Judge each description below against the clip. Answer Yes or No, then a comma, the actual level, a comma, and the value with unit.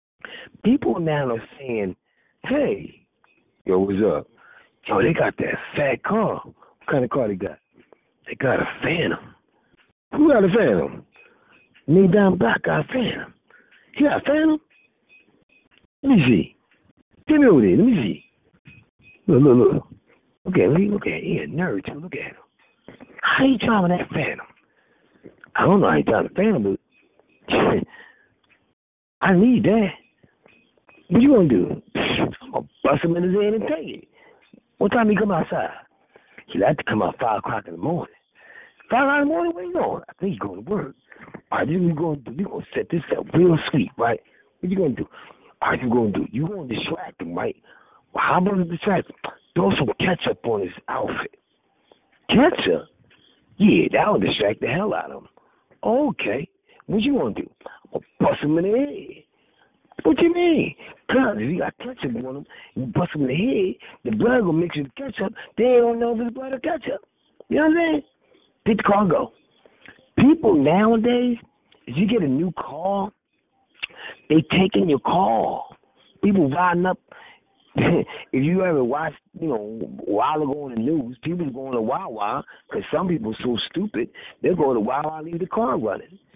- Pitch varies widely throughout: Yes, wide, 8.1 semitones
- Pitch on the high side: Yes, high, 200 Hz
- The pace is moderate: Yes, average, 195 wpm